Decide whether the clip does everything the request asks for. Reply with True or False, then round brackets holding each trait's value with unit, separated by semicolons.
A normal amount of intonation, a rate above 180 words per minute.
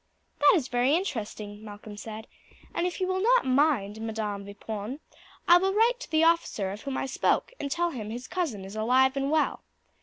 False (7.9 semitones; 200 wpm)